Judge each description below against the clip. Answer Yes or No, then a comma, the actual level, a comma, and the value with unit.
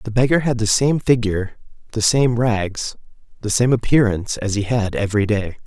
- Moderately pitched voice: No, low, 110 Hz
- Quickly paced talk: No, average, 180 wpm